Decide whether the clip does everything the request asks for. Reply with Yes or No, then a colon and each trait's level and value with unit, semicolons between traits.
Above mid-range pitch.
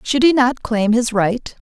Yes: high, 240 Hz